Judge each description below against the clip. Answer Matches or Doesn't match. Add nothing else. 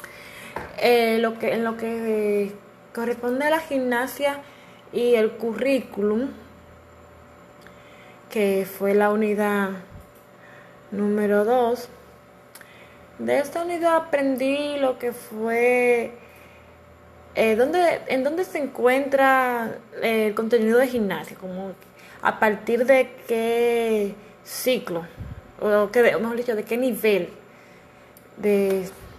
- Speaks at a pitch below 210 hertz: Doesn't match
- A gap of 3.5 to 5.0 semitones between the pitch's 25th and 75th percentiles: Matches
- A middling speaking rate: Doesn't match